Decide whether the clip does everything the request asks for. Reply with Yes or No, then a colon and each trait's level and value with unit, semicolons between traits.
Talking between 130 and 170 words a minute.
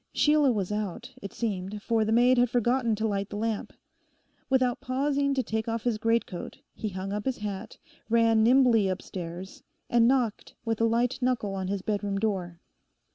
No: average, 180 wpm